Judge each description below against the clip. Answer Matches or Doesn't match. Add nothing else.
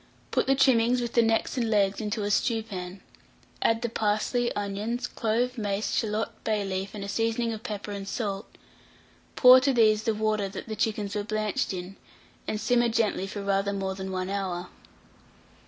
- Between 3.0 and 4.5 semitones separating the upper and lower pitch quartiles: Doesn't match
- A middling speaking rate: Matches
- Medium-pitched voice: Doesn't match